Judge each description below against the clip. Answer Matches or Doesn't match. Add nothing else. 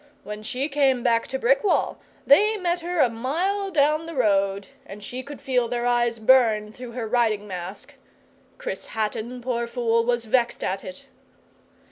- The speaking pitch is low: Doesn't match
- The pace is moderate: Matches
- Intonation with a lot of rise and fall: Doesn't match